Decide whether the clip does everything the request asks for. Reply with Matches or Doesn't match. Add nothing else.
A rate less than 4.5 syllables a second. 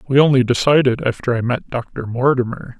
Doesn't match